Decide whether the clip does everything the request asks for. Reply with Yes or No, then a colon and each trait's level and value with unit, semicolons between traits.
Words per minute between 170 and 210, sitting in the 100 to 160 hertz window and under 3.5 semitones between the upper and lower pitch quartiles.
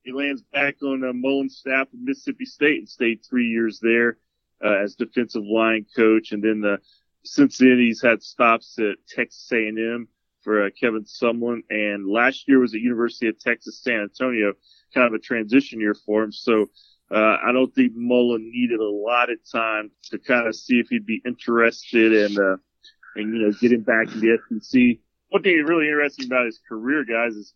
Yes: average, 200 wpm; low, 120 Hz; average, 2.8 semitones